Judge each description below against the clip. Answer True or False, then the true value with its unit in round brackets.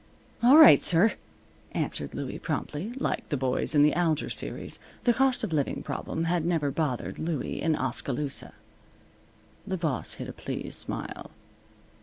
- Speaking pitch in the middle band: True (160 Hz)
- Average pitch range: True (4.4 semitones)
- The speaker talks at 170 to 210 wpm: False (150 wpm)